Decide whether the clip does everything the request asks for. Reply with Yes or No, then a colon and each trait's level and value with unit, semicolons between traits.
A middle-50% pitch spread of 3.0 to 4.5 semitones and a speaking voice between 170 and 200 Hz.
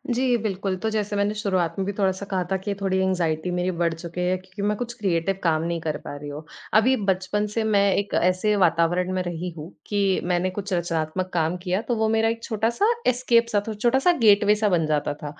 Yes: average, 3.3 semitones; high, 190 Hz